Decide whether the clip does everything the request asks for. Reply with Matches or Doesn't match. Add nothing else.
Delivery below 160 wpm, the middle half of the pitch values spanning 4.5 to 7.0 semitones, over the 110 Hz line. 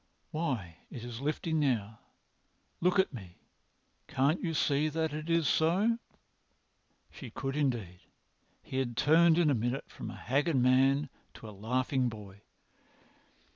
Matches